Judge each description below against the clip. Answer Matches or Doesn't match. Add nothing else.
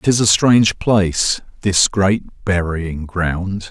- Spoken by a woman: Doesn't match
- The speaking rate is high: Doesn't match